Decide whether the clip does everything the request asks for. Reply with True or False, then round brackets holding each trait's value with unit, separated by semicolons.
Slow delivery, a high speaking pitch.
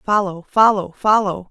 True (120 wpm; 195 Hz)